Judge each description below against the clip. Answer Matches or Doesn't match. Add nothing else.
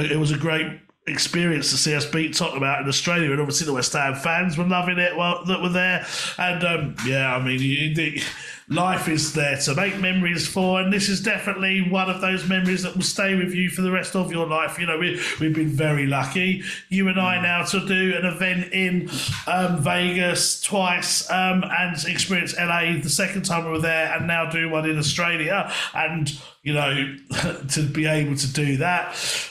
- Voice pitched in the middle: Matches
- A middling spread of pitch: Matches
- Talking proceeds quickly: Matches